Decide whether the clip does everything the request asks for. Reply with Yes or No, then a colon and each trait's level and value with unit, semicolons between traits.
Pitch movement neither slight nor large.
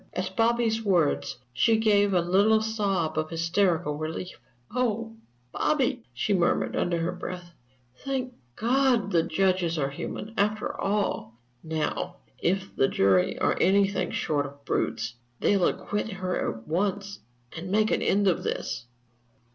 Yes: average, 4.6 semitones